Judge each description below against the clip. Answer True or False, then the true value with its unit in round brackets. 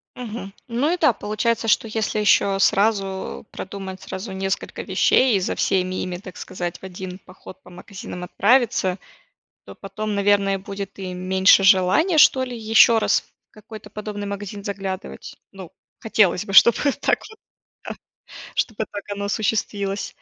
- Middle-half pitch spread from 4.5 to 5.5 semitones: False (2.5 semitones)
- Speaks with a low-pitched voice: False (200 Hz)